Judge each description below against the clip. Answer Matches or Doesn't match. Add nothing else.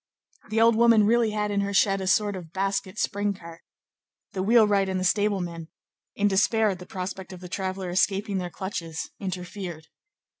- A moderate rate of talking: Matches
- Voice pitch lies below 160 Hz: Doesn't match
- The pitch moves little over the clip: Matches